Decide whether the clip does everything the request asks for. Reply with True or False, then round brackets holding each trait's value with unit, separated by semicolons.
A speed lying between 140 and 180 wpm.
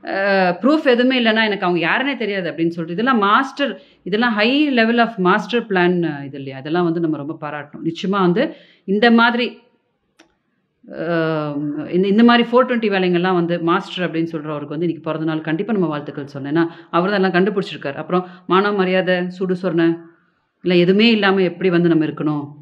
True (160 wpm)